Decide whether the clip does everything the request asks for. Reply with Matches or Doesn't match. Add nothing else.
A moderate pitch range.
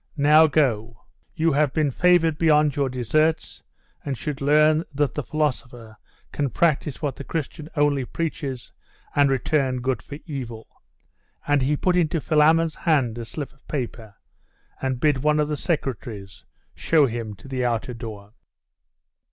Matches